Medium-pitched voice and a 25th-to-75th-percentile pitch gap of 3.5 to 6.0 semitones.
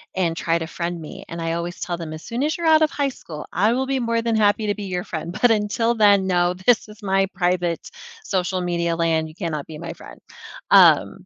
Yes: medium, 180 Hz; average, 4.8 semitones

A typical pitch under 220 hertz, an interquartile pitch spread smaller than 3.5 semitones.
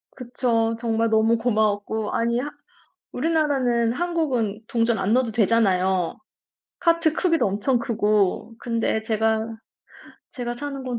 No: high, 230 Hz; narrow, 2.5 semitones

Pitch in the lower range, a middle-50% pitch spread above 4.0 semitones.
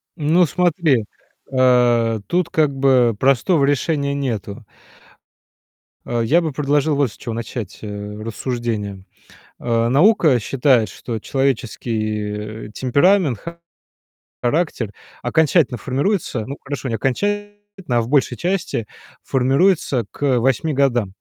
Yes: low, 130 Hz; average, 4.5 semitones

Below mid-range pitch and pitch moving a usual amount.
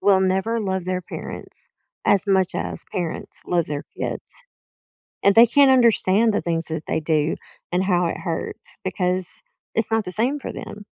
No: high, 190 Hz; average, 4.1 semitones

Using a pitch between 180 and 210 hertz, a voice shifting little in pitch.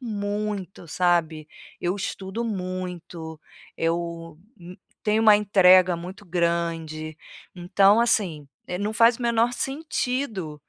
No: medium, 185 Hz; average, 3.9 semitones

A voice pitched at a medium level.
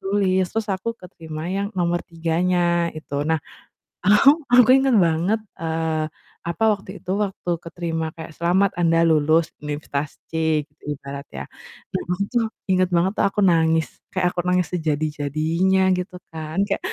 Yes: medium, 170 Hz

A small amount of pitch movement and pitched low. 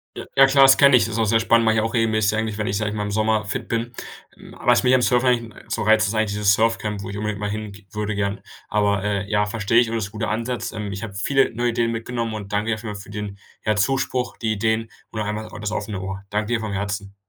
Yes: narrow, 1.8 semitones; low, 110 Hz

